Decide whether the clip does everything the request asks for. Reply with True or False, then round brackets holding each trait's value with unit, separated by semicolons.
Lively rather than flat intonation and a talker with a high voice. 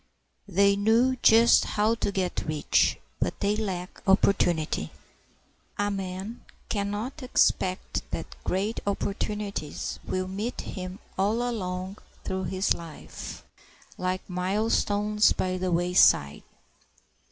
False (2.4 semitones; 195 Hz)